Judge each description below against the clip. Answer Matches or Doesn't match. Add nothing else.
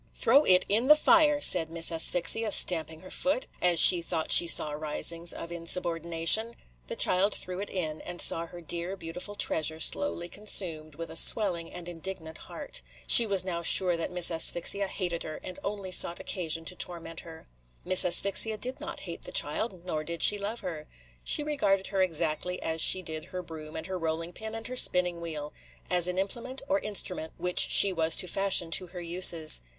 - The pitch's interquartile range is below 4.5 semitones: Matches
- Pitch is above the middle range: Doesn't match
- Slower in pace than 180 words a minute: Doesn't match